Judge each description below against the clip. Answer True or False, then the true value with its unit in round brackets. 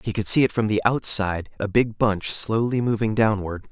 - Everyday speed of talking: False (210 wpm)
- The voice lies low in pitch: True (110 Hz)